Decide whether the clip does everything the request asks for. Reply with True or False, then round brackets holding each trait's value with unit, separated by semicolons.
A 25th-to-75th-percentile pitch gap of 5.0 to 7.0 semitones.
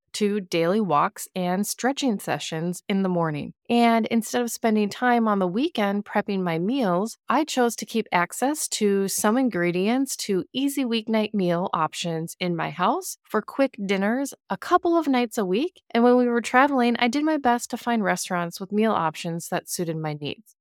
True (5.3 semitones)